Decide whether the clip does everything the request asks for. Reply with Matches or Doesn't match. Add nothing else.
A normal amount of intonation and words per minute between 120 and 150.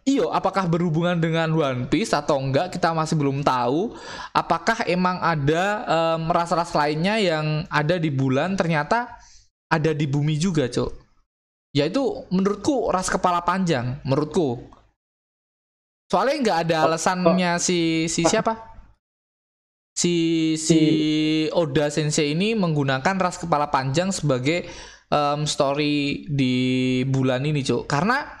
Matches